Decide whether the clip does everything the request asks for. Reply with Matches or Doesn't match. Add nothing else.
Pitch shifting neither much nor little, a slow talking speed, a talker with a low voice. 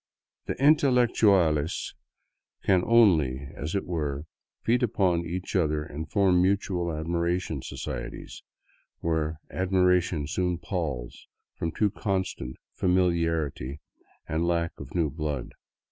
Matches